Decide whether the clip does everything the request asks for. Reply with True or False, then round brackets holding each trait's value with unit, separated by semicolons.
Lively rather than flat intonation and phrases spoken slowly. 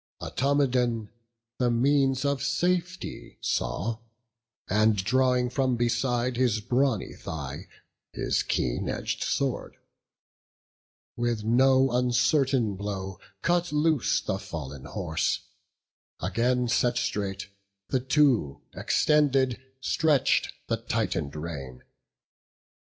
False (4.8 semitones; 95 wpm)